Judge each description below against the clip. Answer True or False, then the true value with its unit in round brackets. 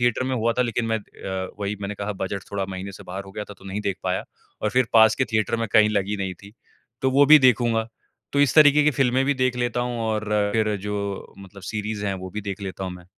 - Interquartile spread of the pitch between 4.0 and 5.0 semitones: False (3.6 semitones)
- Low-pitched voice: True (105 Hz)